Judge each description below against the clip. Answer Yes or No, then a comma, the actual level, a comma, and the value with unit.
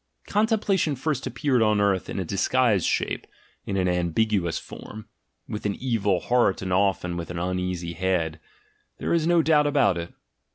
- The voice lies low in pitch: Yes, low, 100 Hz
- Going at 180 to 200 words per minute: No, average, 165 wpm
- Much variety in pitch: Yes, wide, 6.3 semitones